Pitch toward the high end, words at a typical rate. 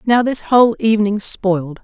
Yes: high, 210 Hz; average, 165 wpm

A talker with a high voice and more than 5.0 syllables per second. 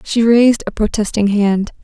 No: high, 215 Hz; 4.9 syllables/s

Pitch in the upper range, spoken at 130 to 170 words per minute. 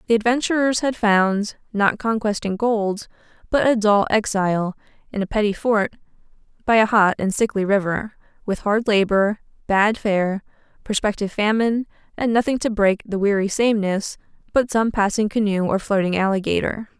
Yes: high, 210 Hz; average, 150 wpm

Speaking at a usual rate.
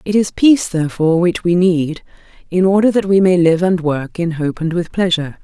No: fast, 220 wpm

